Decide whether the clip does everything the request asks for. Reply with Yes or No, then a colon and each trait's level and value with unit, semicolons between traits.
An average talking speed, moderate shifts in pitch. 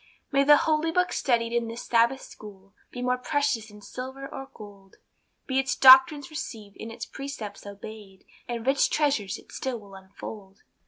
Yes: average, 170 wpm; average, 4.7 semitones